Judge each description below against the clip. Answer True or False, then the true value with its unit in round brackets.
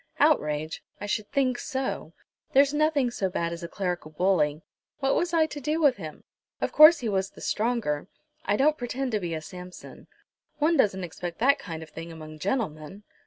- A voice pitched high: True (205 Hz)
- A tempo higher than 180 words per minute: True (190 wpm)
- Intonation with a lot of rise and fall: True (8.6 semitones)